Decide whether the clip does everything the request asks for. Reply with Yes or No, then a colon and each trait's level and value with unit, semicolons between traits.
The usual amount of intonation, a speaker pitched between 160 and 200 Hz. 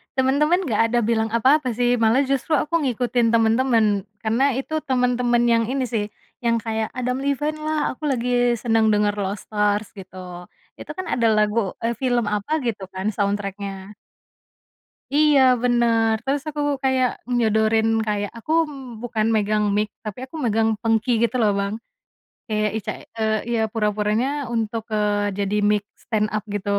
No: average, 3.1 semitones; high, 225 Hz